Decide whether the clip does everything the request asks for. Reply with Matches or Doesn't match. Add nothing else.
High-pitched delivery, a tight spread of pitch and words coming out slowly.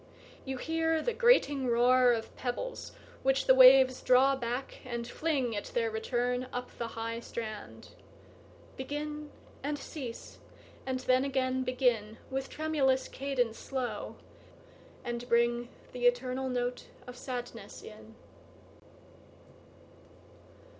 Matches